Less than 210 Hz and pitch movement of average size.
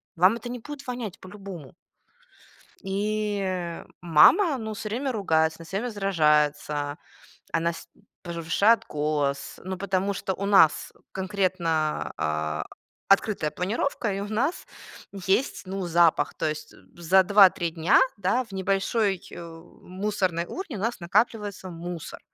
Yes: high, 190 Hz; average, 4.0 semitones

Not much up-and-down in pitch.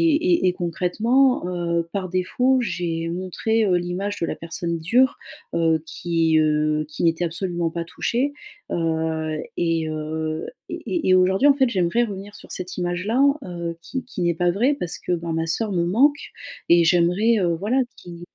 No: average, 3.7 semitones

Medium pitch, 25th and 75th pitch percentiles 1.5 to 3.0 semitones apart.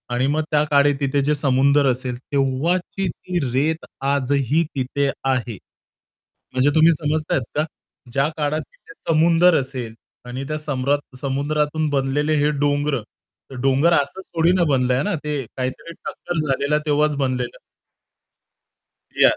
Yes: medium, 145 Hz; narrow, 2.5 semitones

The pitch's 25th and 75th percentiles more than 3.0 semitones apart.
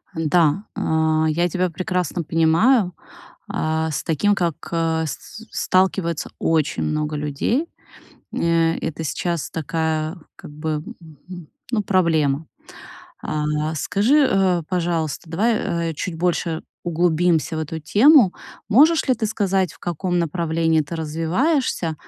No: average, 2.7 semitones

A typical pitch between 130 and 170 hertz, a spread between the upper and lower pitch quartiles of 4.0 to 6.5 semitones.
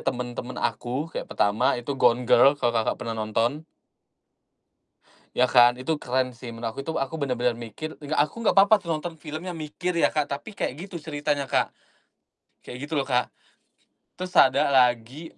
Yes: low, 135 Hz; average, 4.3 semitones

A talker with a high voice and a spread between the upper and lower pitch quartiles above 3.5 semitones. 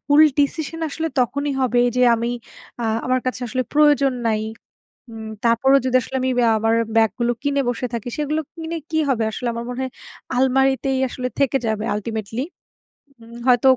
No: very high, 255 Hz; average, 3.2 semitones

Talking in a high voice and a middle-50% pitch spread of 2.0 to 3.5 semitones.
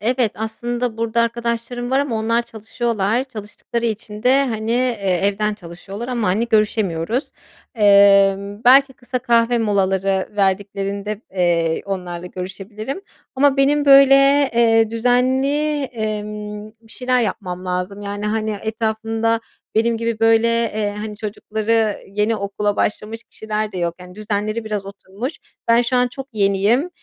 Yes: high, 220 Hz; average, 2.8 semitones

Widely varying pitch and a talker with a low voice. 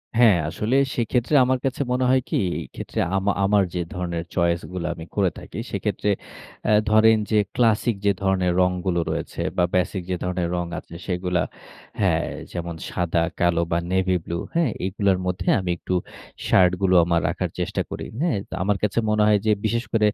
No: average, 3.3 semitones; very low, 95 Hz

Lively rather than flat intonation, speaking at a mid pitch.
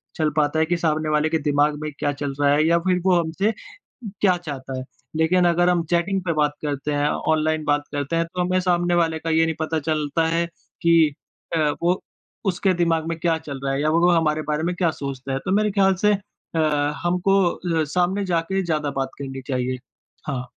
No: average, 2.9 semitones; medium, 160 Hz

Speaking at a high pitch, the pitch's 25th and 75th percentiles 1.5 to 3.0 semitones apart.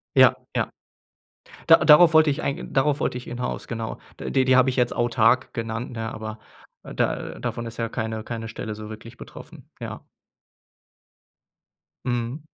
No: low, 120 Hz; narrow, 2.6 semitones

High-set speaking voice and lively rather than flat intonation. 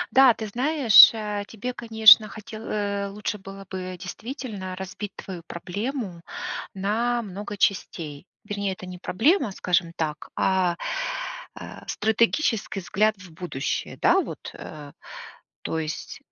No: high, 200 Hz; average, 3.3 semitones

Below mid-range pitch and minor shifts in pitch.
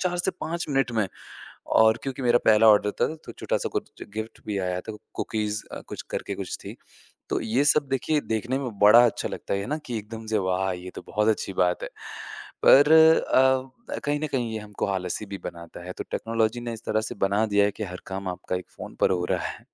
No: low, 110 Hz; average, 3.6 semitones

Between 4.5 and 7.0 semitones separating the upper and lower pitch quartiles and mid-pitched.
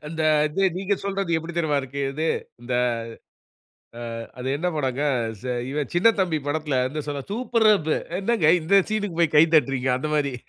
Yes: average, 5.3 semitones; medium, 155 Hz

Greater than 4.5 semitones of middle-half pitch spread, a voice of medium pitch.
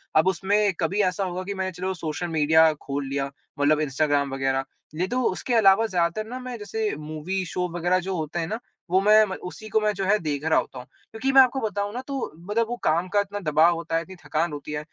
Yes: average, 4.9 semitones; medium, 180 Hz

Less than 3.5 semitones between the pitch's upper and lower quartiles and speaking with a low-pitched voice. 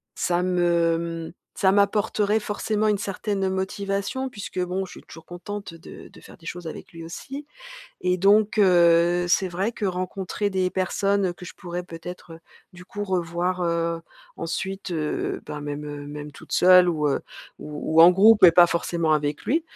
No: average, 2.9 semitones; medium, 180 Hz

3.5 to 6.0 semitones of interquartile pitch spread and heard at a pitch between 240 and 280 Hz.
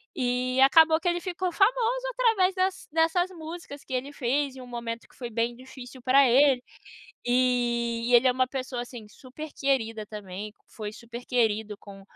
Yes: average, 5.1 semitones; very high, 255 Hz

